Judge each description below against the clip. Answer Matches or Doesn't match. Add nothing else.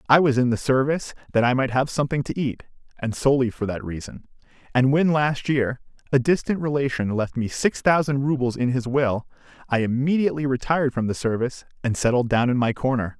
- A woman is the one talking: Doesn't match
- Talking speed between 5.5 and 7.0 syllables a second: Matches